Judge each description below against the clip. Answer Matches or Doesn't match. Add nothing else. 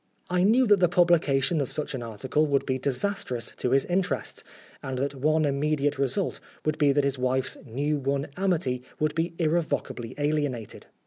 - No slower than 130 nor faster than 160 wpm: Doesn't match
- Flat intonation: Doesn't match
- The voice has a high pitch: Doesn't match